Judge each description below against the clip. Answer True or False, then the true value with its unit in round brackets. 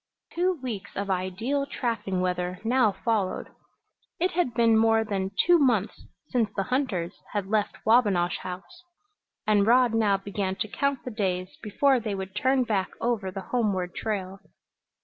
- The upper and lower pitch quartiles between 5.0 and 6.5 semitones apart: False (4.4 semitones)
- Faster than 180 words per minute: False (155 wpm)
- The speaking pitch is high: True (215 Hz)